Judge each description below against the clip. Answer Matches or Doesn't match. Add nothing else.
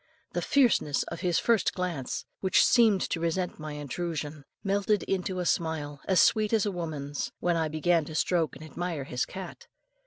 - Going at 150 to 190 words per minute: Matches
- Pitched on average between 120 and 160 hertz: Doesn't match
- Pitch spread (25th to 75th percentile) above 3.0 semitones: Matches